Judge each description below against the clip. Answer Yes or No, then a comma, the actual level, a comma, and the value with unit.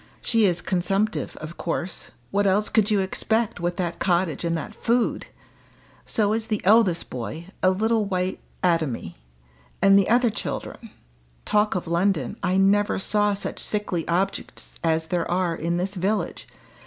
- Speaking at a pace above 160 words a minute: No, average, 155 wpm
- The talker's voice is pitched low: No, high, 190 Hz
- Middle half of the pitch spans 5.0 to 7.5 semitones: No, average, 3.4 semitones